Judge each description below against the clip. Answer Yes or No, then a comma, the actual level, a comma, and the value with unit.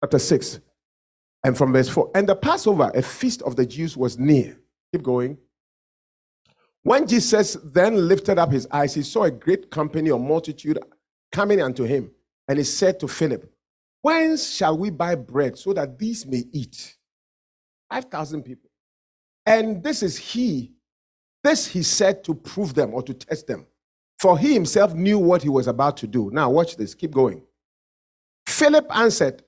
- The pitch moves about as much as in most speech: No, wide, 7.6 semitones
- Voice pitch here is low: No, medium, 155 Hz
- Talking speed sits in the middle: Yes, average, 170 wpm